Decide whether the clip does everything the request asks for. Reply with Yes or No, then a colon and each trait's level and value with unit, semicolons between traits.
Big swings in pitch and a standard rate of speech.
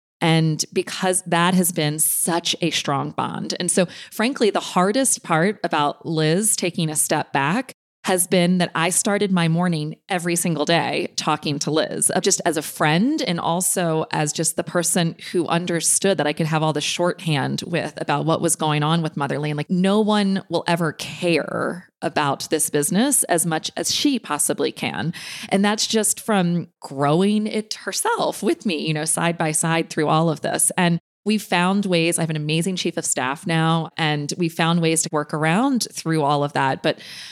No: average, 3.0 semitones; average, 190 wpm